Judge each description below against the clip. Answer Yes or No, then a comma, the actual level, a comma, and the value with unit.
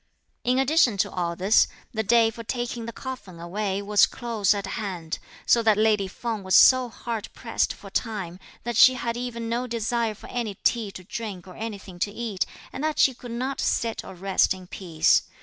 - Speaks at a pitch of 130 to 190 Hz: No, high, 220 Hz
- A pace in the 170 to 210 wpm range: Yes, average, 200 wpm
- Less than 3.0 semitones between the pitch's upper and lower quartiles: No, average, 3.5 semitones